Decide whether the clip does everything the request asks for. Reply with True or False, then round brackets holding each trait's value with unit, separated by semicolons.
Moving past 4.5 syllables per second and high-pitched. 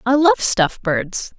False (4.1 syllables/s; 230 Hz)